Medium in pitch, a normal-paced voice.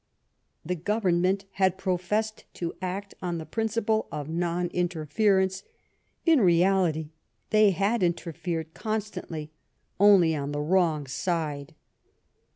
No: medium, 180 Hz; slow, 115 wpm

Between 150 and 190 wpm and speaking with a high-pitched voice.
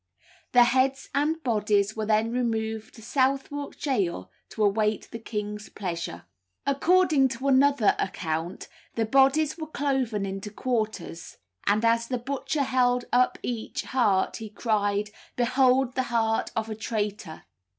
No: average, 140 wpm; high, 230 Hz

